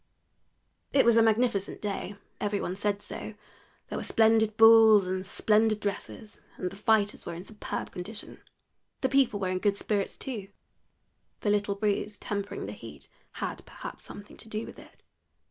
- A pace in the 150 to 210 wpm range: Yes, average, 165 wpm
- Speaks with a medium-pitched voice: No, high, 210 Hz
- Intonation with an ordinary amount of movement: No, narrow, 1.7 semitones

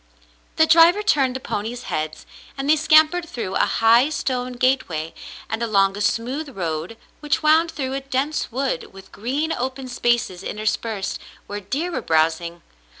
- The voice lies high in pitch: Yes, very high, 250 Hz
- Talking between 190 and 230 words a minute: No, average, 155 wpm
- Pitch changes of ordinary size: No, wide, 6.3 semitones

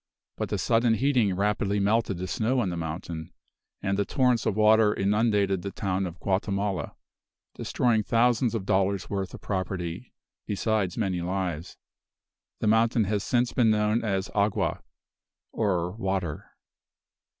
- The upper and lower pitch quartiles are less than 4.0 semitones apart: Yes, average, 2.9 semitones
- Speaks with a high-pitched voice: No, low, 100 Hz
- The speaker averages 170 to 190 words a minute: No, average, 140 wpm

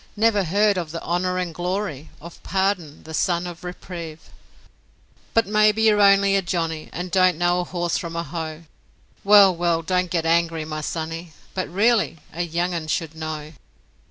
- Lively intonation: No, average, 2.7 semitones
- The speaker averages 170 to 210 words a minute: Yes, average, 175 wpm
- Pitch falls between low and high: Yes, medium, 175 Hz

